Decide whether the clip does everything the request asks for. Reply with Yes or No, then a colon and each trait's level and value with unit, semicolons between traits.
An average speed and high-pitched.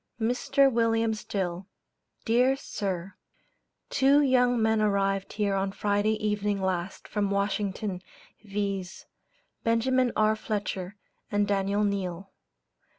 No: slow, 105 wpm; high, 205 Hz